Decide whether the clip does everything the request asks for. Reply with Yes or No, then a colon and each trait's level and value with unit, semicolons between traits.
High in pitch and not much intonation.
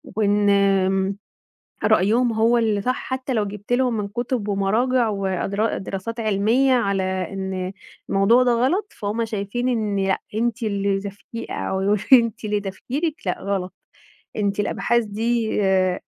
No: high, 210 Hz; average, 3.2 semitones